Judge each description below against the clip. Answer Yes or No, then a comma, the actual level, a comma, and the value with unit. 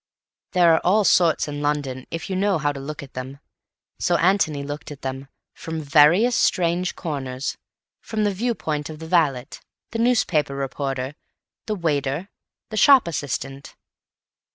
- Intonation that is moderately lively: Yes, average, 4.6 semitones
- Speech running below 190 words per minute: Yes, average, 155 wpm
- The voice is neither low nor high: Yes, medium, 155 Hz